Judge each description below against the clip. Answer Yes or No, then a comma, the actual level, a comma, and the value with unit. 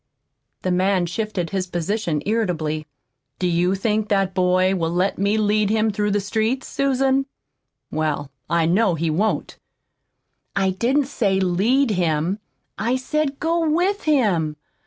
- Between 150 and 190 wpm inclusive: No, average, 140 wpm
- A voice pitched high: Yes, high, 200 Hz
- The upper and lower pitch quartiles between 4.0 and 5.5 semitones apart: Yes, average, 4.5 semitones